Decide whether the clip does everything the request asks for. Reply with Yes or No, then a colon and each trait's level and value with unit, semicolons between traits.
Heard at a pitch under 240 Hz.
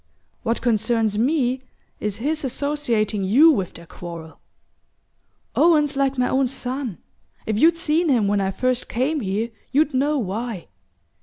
No: very high, 250 Hz